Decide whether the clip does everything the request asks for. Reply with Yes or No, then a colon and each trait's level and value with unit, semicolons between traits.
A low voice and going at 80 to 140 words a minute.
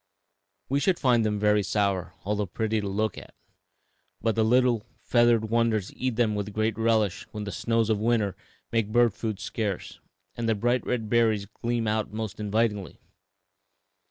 No: low, 110 Hz; average, 165 wpm